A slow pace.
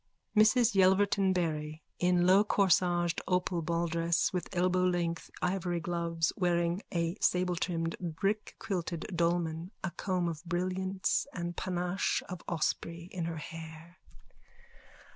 Yes: slow, 105 wpm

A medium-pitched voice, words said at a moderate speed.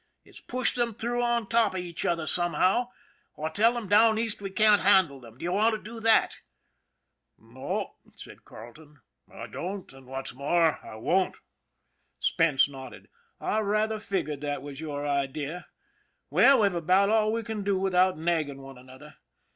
Yes: medium, 180 Hz; average, 180 wpm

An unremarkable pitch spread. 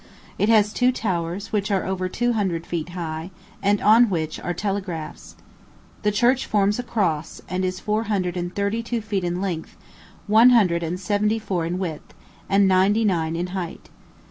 Yes: average, 3.3 semitones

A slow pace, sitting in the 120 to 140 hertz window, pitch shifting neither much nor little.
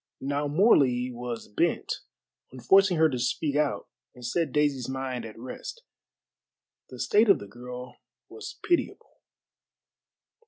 Yes: slow, 130 wpm; low, 135 Hz; average, 4.5 semitones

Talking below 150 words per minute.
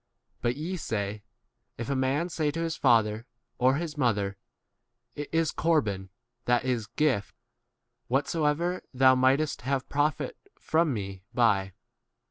Yes: slow, 135 wpm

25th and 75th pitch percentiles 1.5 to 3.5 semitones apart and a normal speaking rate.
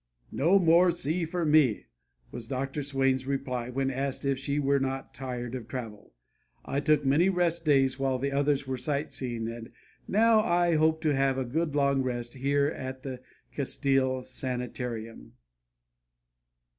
Yes: average, 2.7 semitones; average, 155 wpm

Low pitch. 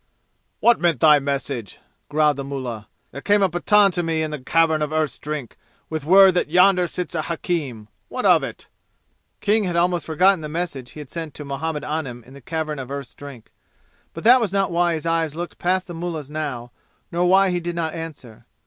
No: medium, 160 Hz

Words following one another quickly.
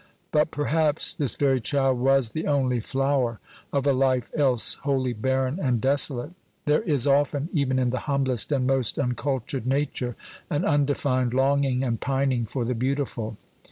No: average, 160 wpm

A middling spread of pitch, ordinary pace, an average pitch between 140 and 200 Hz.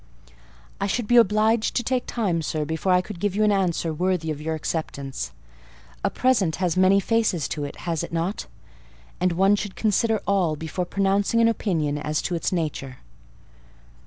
Yes: average, 4.4 semitones; average, 180 wpm; medium, 185 Hz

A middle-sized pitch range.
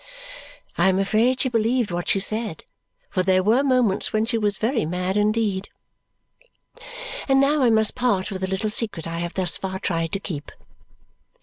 Yes: average, 3.5 semitones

